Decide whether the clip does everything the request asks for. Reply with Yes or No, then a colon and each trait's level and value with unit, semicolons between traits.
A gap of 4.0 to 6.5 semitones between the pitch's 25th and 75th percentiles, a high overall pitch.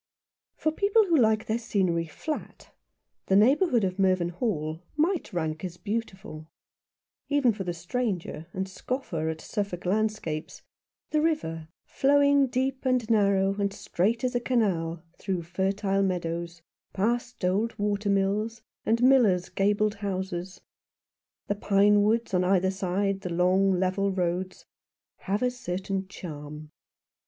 Yes: average, 4.3 semitones; high, 195 Hz